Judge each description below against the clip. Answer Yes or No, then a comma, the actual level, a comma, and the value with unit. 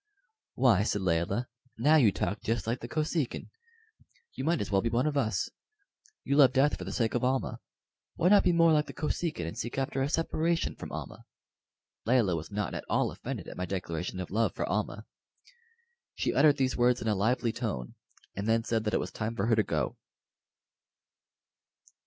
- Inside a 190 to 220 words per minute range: Yes, average, 195 wpm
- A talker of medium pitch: No, low, 115 Hz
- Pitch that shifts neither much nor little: No, wide, 5.7 semitones